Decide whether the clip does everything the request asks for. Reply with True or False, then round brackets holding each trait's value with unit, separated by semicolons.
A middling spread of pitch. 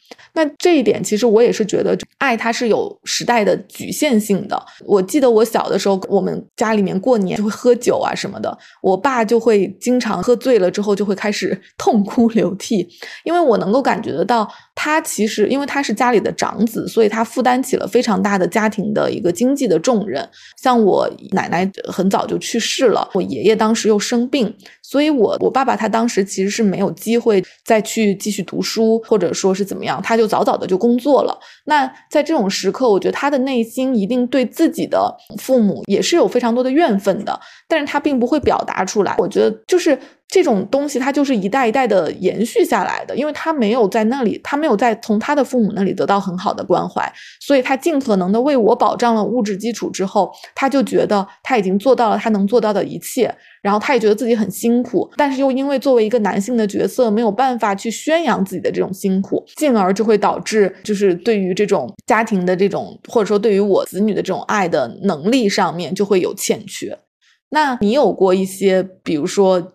True (4.6 semitones)